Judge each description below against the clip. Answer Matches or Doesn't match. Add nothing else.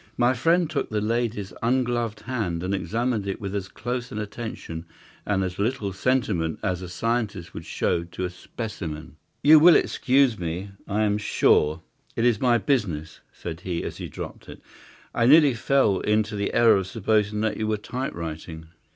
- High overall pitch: Doesn't match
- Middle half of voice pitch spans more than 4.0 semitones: Matches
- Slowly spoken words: Doesn't match